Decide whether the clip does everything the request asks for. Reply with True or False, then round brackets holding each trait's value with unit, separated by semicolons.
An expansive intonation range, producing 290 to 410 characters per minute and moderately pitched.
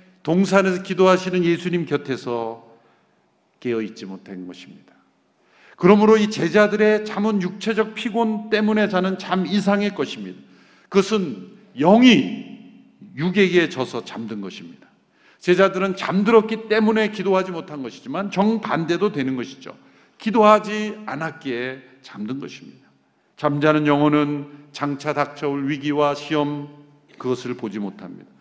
True (6.6 semitones; 295 characters per minute; 180 Hz)